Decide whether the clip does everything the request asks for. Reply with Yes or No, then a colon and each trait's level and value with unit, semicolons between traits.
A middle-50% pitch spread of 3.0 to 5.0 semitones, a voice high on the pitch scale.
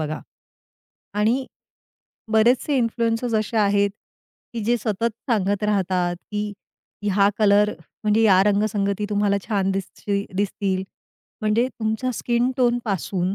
No: narrow, 2.4 semitones; high, 210 Hz